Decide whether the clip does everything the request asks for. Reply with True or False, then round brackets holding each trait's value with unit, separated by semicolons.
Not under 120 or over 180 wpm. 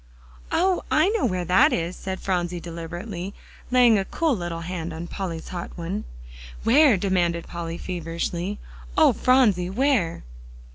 True (140 wpm)